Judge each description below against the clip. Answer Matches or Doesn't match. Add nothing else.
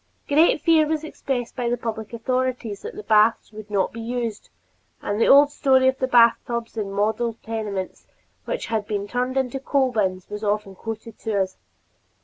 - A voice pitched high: Matches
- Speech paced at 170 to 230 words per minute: Matches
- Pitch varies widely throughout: Doesn't match